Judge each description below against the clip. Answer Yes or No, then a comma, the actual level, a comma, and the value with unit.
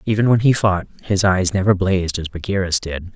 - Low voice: Yes, very low, 95 Hz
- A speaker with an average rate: No, fast, 210 wpm